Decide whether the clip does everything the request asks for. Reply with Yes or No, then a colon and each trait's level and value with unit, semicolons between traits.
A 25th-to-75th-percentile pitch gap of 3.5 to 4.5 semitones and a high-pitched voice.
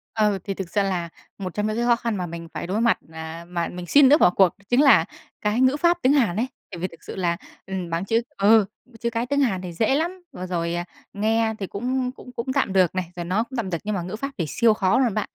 No: average, 4.9 semitones; high, 210 Hz